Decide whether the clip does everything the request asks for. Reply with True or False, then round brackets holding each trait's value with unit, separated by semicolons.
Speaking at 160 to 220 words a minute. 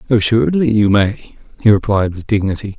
False (150 wpm)